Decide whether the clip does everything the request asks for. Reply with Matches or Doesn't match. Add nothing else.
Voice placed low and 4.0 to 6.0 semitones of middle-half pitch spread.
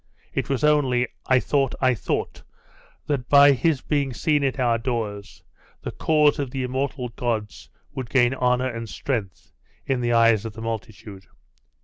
Doesn't match